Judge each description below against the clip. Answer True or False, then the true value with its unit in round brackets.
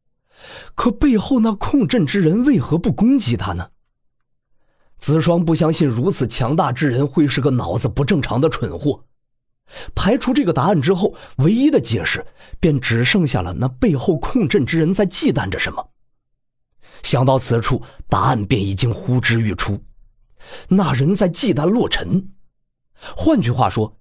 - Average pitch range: False (7.5 semitones)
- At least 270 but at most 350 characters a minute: False (230 characters per minute)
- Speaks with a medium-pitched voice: True (145 Hz)